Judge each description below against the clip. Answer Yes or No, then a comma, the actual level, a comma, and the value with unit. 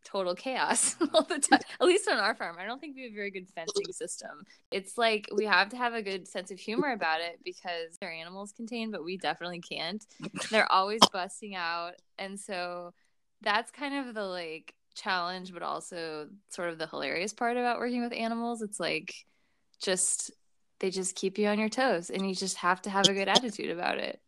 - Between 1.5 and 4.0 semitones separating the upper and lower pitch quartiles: No, average, 4.5 semitones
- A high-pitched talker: Yes, high, 195 Hz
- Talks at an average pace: No, fast, 210 wpm